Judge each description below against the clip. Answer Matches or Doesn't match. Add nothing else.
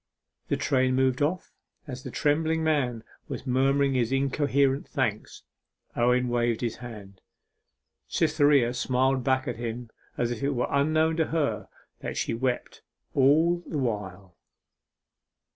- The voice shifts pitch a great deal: Doesn't match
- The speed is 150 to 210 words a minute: Doesn't match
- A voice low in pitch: Matches